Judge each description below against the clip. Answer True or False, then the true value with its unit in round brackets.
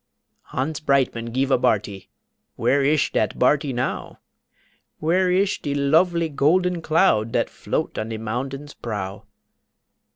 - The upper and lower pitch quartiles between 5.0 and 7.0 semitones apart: True (5.5 semitones)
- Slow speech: True (130 wpm)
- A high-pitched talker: False (140 Hz)